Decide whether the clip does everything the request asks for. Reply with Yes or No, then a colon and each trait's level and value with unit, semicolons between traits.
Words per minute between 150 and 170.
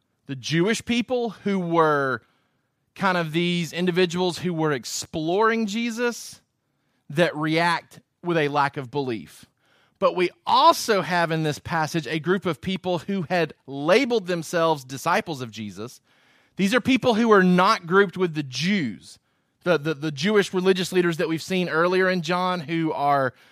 Yes: average, 160 wpm